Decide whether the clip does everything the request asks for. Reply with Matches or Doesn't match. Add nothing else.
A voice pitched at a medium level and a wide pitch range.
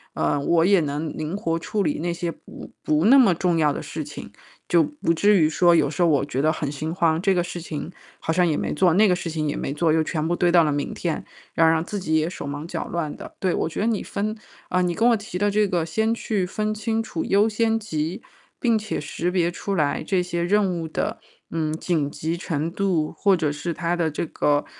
Doesn't match